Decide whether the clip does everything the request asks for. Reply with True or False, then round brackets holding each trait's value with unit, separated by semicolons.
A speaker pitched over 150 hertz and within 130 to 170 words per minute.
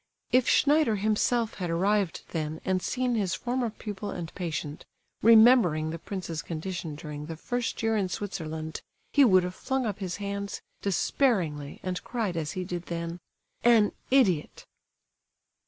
True (190 Hz; 150 wpm)